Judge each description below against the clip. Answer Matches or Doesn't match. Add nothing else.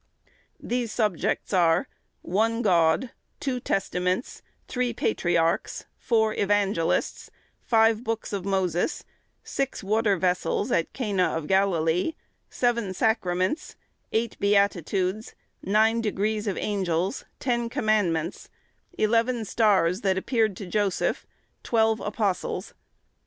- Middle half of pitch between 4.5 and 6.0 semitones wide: Doesn't match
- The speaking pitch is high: Matches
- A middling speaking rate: Doesn't match